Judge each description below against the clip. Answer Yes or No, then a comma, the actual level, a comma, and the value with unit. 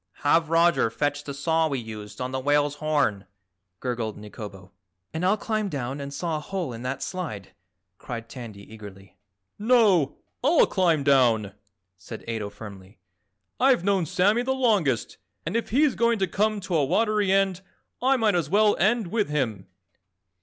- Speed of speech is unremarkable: Yes, average, 165 wpm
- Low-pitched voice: No, medium, 155 Hz